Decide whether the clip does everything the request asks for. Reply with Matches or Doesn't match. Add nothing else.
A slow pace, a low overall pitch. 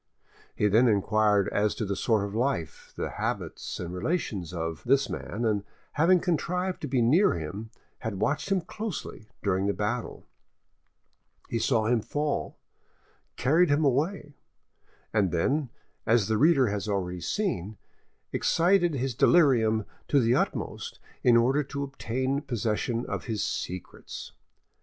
Doesn't match